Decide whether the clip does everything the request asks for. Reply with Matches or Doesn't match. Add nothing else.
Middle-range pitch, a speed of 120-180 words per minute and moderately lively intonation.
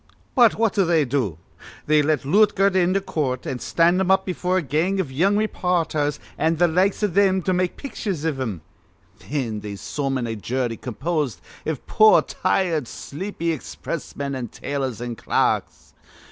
Doesn't match